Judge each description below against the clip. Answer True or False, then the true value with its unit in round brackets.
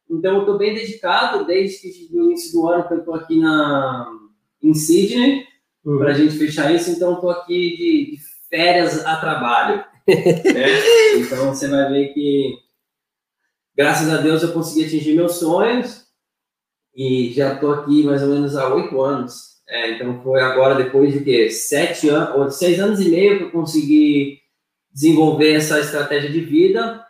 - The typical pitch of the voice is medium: True (155 Hz)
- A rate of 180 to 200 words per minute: False (165 wpm)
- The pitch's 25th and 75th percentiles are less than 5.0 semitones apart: False (5.5 semitones)